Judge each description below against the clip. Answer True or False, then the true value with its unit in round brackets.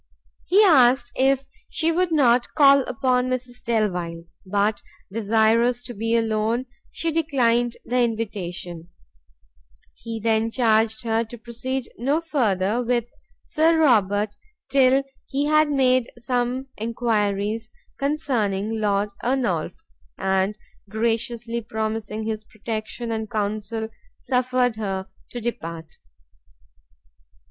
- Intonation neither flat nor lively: True (3.0 semitones)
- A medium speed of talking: False (110 wpm)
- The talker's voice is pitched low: False (230 Hz)